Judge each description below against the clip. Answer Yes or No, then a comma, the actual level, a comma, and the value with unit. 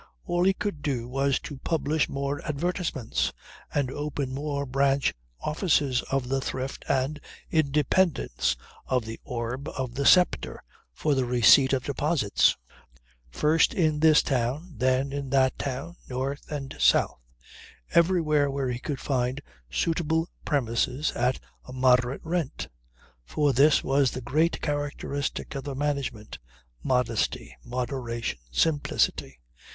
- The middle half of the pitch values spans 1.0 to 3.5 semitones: Yes, average, 3.0 semitones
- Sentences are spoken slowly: Yes, slow, 130 wpm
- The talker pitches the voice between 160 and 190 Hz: No, medium, 140 Hz